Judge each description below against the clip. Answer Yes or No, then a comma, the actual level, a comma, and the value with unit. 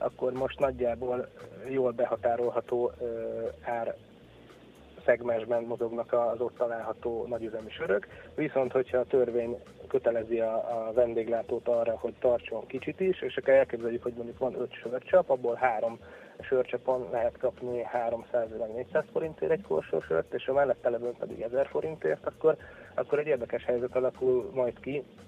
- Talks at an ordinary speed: Yes, average, 135 wpm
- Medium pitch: No, low, 120 Hz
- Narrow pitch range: Yes, narrow, 1.9 semitones